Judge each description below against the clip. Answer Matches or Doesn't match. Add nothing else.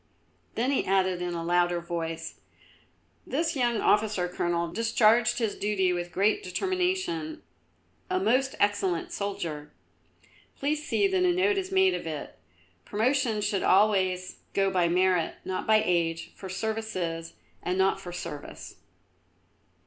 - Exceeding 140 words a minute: Doesn't match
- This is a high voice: Matches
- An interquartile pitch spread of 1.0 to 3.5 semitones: Doesn't match